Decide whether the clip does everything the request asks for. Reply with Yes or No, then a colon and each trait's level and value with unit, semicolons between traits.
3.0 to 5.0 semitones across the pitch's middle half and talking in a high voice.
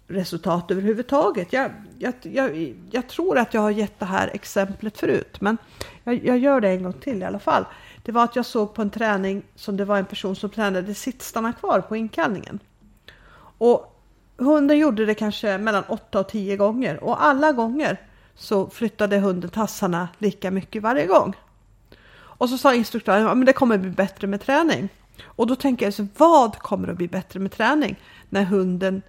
Yes: average, 3.7 semitones; high, 215 Hz